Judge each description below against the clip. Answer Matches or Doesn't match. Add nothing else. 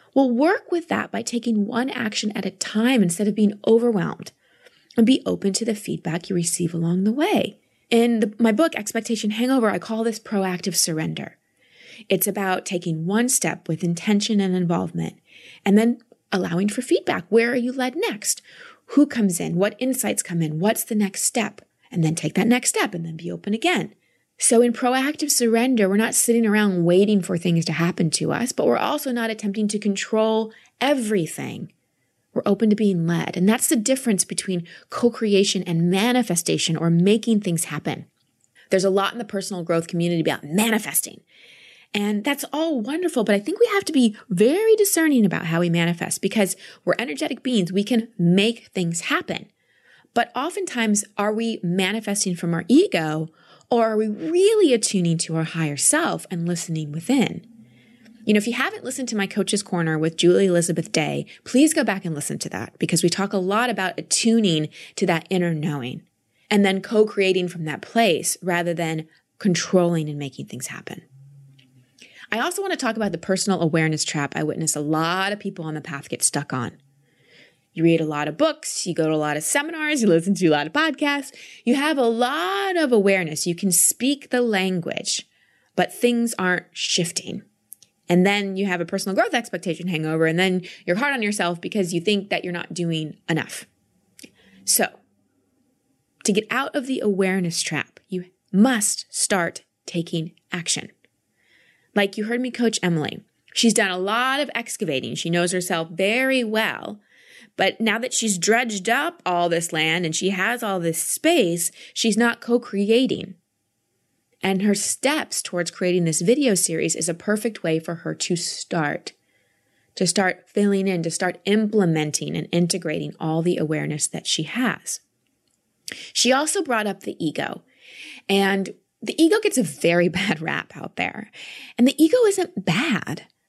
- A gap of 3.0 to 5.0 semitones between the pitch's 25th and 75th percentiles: Doesn't match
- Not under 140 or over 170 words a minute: Doesn't match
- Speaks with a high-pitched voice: Matches